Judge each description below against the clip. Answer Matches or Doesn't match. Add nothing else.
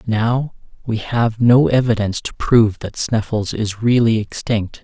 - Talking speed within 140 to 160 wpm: Matches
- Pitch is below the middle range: Matches